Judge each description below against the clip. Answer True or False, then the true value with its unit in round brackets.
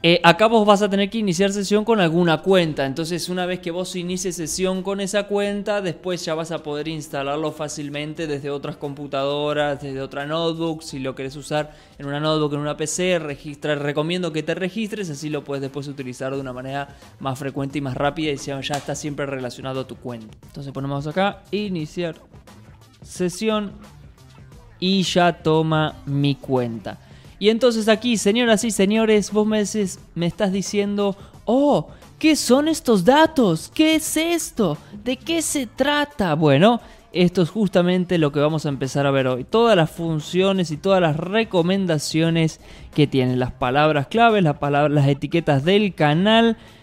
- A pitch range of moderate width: False (5.8 semitones)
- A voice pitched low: False (165 Hz)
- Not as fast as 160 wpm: False (175 wpm)